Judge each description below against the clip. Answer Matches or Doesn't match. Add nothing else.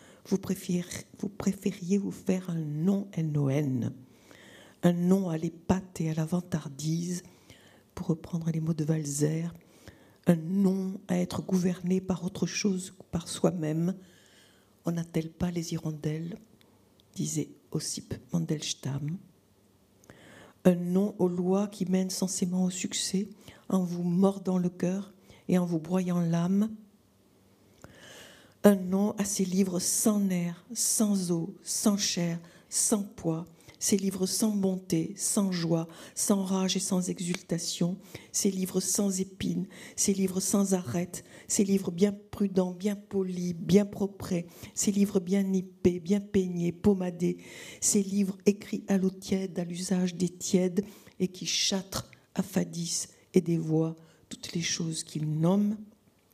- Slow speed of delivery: Matches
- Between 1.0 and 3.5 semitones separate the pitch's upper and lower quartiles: Matches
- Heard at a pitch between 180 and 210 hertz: Matches